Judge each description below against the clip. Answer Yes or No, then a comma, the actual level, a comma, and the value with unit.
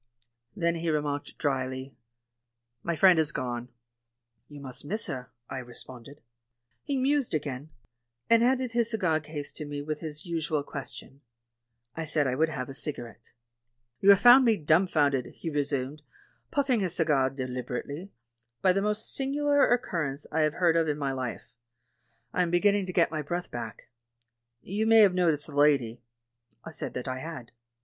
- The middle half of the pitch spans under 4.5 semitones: No, average, 5.2 semitones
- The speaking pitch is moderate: Yes, medium, 155 Hz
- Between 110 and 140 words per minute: No, average, 165 wpm